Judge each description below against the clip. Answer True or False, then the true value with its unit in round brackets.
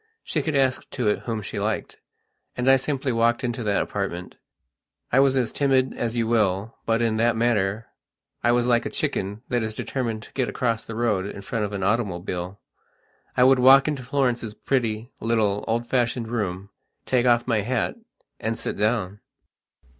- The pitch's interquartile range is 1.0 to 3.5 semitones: True (2.9 semitones)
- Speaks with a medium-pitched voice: False (115 Hz)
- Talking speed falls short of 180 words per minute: False (185 wpm)